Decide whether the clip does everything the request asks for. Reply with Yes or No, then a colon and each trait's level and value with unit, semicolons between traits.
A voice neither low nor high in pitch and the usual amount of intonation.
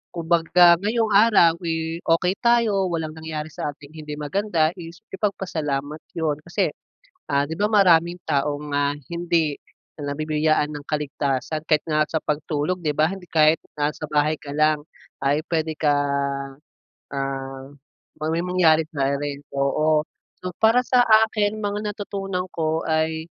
Yes: medium, 160 Hz; average, 3.3 semitones